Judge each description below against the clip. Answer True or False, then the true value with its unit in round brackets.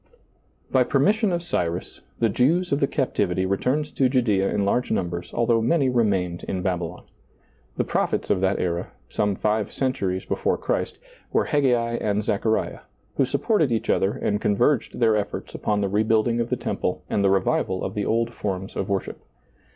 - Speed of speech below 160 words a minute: False (185 wpm)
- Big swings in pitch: False (4.4 semitones)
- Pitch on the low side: True (105 Hz)